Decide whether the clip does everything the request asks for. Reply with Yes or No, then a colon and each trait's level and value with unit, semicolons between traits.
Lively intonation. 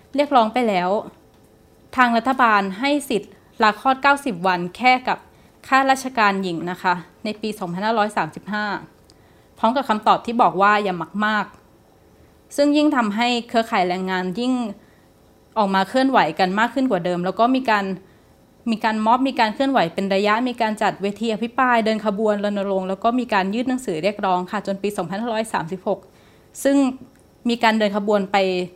No: average, 3.8 semitones